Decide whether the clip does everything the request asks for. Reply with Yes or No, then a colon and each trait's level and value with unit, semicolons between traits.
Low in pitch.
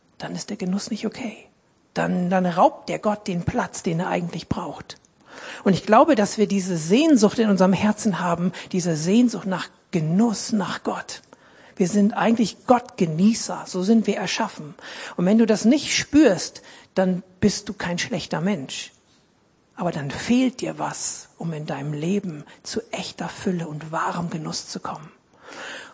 No: high, 195 Hz